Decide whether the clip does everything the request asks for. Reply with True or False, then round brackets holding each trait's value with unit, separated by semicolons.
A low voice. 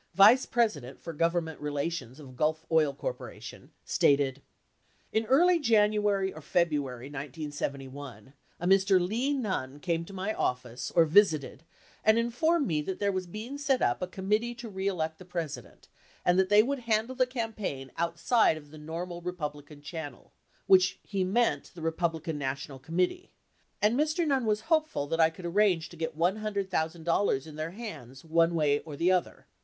False (175 Hz)